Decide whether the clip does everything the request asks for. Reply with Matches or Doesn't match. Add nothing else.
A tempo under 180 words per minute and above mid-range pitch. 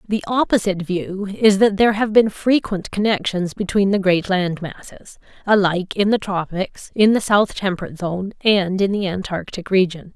Matches